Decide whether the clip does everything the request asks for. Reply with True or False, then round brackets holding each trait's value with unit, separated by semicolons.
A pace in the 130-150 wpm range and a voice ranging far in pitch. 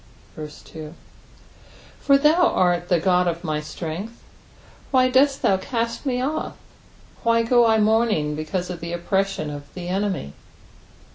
True (140 wpm; 5.7 semitones)